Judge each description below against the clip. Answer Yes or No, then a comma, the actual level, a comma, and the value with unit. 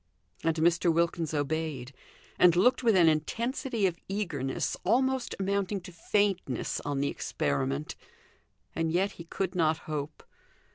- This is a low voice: No, medium, 170 Hz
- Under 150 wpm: Yes, slow, 135 wpm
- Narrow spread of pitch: No, average, 4.4 semitones